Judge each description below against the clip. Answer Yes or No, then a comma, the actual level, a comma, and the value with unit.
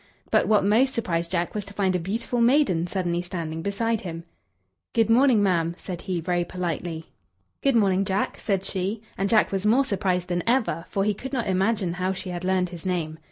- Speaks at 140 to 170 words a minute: No, fast, 205 wpm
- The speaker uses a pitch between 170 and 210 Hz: Yes, high, 190 Hz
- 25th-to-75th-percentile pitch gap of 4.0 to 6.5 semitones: No, average, 3.4 semitones